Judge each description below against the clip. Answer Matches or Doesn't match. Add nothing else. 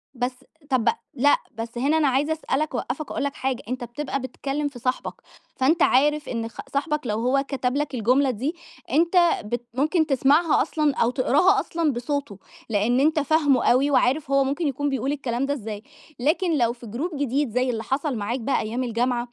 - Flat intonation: Doesn't match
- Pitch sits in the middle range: Doesn't match